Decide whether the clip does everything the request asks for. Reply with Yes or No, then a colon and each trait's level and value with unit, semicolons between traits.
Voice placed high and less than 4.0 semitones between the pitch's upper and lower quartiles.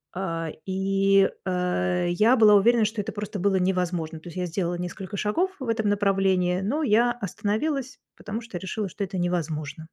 Yes: high, 195 Hz; average, 3.1 semitones